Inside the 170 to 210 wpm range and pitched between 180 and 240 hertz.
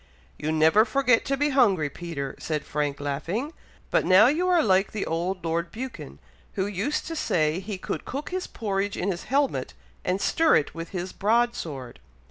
Yes: average, 185 wpm; high, 190 Hz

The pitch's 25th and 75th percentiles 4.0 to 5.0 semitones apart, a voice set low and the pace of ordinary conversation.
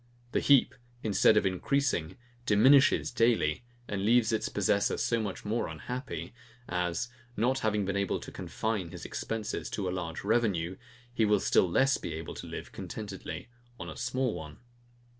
Yes: average, 4.5 semitones; low, 105 Hz; average, 160 wpm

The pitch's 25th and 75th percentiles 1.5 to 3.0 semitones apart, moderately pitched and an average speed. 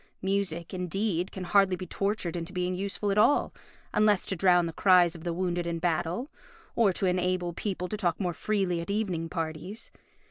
Yes: narrow, 2.5 semitones; medium, 180 Hz; average, 185 wpm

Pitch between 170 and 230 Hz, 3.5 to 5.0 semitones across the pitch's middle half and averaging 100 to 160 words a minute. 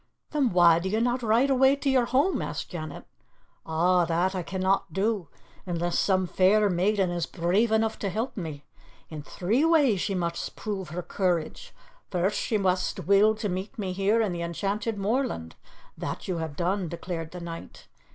No: high, 190 Hz; average, 4.0 semitones; average, 180 wpm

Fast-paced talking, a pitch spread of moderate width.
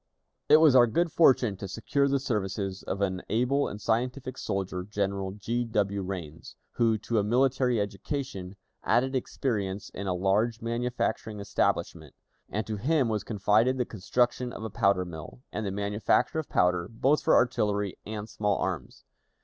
No: average, 165 wpm; average, 4.0 semitones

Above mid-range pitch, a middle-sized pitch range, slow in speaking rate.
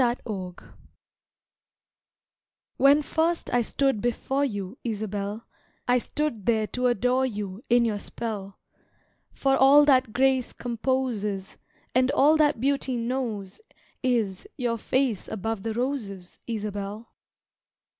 Yes: high, 235 Hz; average, 4.0 semitones; slow, 115 wpm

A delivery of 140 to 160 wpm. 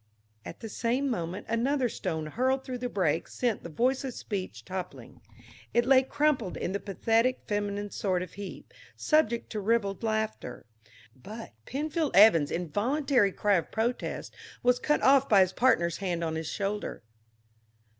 Yes: average, 155 wpm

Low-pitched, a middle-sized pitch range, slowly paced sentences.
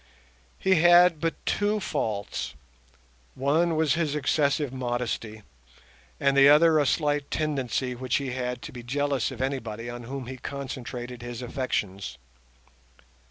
Yes: low, 130 Hz; average, 3.5 semitones; slow, 130 wpm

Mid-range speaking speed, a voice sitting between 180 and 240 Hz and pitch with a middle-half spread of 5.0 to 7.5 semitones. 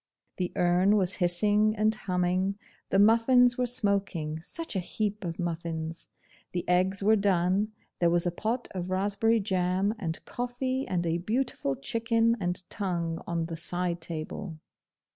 No: average, 150 wpm; high, 190 Hz; average, 3.7 semitones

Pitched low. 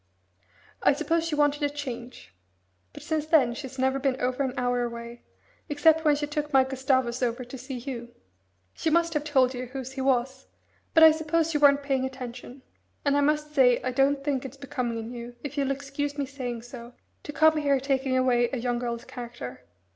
No: very high, 265 Hz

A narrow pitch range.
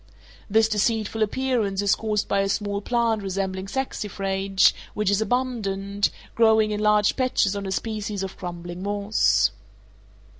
Yes: narrow, 2.1 semitones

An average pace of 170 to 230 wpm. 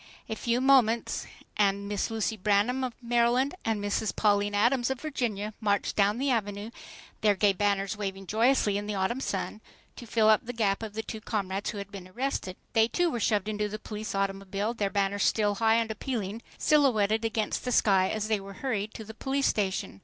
Yes: average, 200 wpm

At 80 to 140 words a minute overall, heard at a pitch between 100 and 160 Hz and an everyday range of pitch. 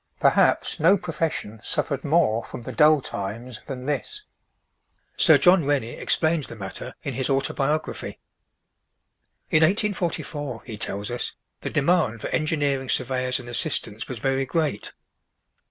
Yes: slow, 135 wpm; low, 135 Hz; average, 4.7 semitones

